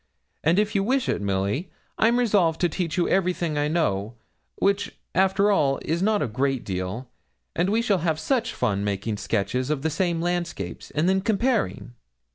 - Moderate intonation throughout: No, wide, 7.6 semitones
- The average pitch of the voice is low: No, medium, 165 Hz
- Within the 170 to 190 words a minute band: Yes, average, 180 wpm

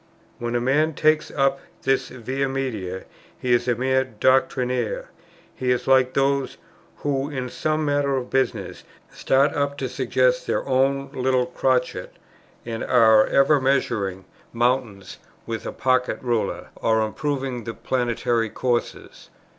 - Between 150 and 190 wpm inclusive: No, average, 140 wpm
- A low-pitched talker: Yes, low, 130 Hz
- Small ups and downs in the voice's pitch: Yes, narrow, 2.3 semitones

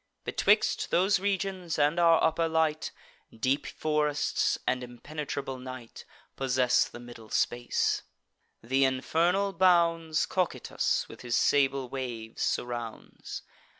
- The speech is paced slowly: Yes, slow, 110 wpm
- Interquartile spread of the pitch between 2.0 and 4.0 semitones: No, average, 4.8 semitones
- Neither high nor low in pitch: Yes, medium, 145 Hz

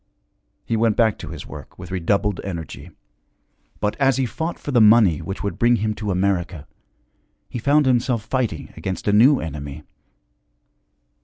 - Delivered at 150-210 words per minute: Yes, average, 160 wpm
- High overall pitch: No, low, 105 Hz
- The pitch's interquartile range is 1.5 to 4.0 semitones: No, average, 4.7 semitones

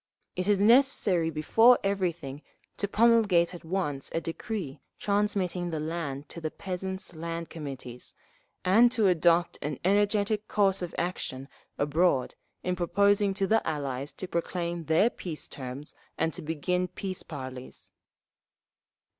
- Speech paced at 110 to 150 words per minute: Yes, average, 140 wpm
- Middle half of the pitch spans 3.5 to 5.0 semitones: Yes, average, 4.4 semitones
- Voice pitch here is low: No, medium, 175 Hz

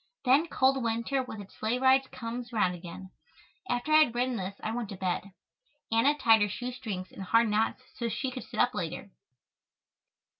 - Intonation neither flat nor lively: Yes, average, 4.0 semitones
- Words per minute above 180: Yes, average, 190 wpm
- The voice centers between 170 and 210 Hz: No, high, 230 Hz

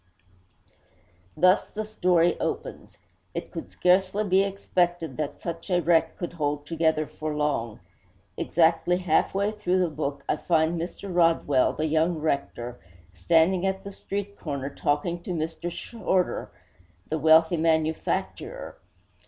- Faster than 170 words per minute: No, slow, 135 wpm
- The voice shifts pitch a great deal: No, average, 2.9 semitones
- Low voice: No, medium, 165 Hz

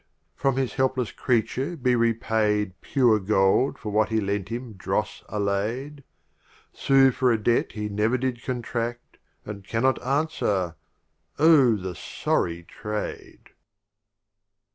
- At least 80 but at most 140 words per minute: Yes, slow, 135 wpm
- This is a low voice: Yes, low, 115 Hz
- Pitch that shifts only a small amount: No, average, 3.8 semitones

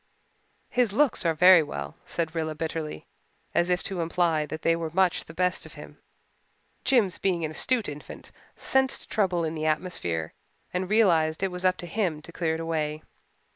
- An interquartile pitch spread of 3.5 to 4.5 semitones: No, average, 2.9 semitones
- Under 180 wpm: No, average, 185 wpm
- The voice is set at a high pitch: No, medium, 170 Hz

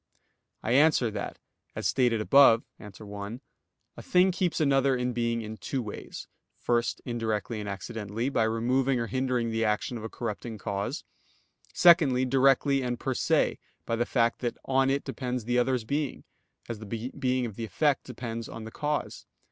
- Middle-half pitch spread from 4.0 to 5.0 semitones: No, average, 2.9 semitones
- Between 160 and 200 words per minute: Yes, average, 175 wpm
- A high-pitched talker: No, low, 120 Hz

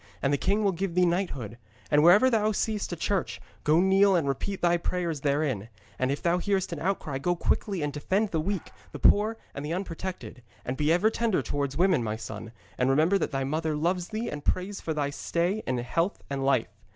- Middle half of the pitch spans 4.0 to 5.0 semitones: No, wide, 5.5 semitones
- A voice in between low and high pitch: Yes, medium, 170 Hz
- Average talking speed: No, fast, 215 wpm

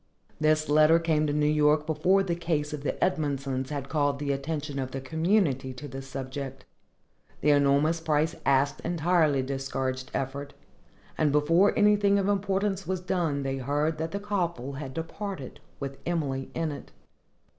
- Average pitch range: Yes, average, 3.3 semitones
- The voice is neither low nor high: Yes, medium, 150 Hz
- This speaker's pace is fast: No, average, 160 wpm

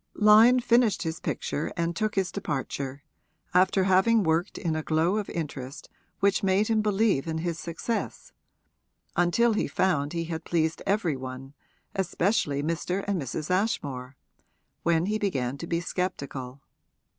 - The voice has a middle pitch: Yes, medium, 170 Hz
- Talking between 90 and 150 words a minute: Yes, average, 145 wpm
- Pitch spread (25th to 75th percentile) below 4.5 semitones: No, average, 4.9 semitones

